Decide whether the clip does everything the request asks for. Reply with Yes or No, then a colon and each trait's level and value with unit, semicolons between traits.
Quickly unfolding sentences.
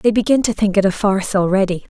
Yes: fast, 240 wpm